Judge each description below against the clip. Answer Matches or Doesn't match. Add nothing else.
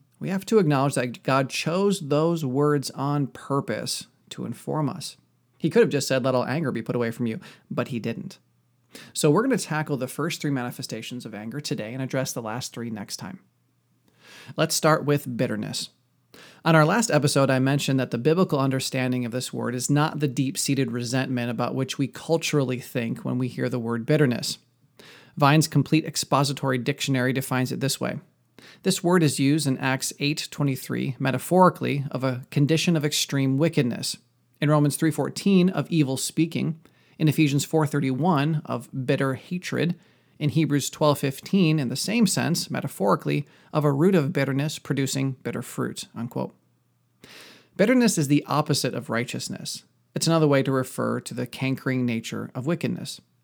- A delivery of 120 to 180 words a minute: Matches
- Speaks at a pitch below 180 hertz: Matches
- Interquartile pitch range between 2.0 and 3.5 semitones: Matches